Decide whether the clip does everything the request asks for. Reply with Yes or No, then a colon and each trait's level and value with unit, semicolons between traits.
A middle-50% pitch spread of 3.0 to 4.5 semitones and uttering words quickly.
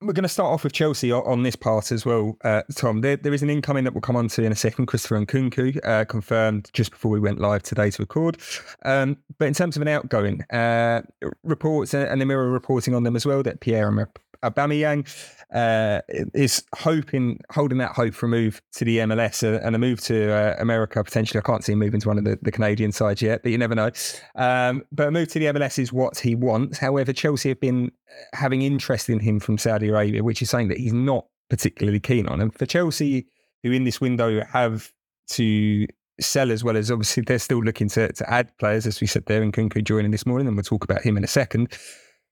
Yes: average, 3.6 semitones; fast, 235 wpm